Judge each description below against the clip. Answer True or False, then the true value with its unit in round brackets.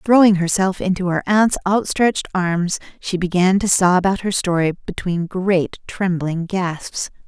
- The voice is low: False (185 Hz)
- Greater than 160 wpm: False (150 wpm)